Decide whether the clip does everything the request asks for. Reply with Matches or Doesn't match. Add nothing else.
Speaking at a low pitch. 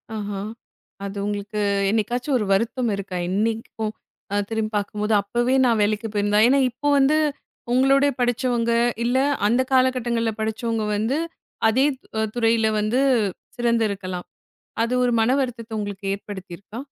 Doesn't match